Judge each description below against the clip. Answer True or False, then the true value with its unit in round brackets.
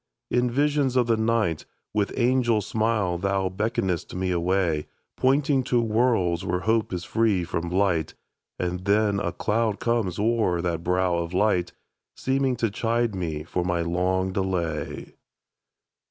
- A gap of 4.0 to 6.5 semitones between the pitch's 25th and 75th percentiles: True (4.5 semitones)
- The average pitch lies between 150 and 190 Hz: False (100 Hz)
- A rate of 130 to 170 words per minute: True (145 wpm)